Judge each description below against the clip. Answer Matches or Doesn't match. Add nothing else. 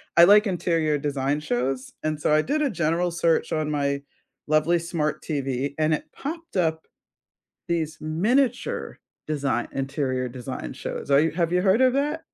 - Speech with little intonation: Doesn't match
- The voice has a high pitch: Doesn't match